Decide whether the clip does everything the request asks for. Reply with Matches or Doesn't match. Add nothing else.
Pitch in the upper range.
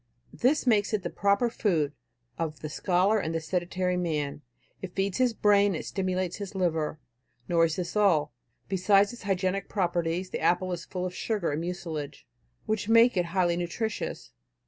Doesn't match